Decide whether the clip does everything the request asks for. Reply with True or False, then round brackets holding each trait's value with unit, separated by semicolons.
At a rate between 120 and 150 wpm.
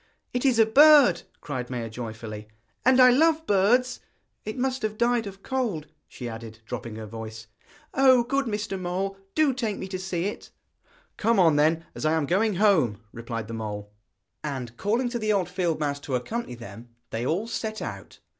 False (185 wpm)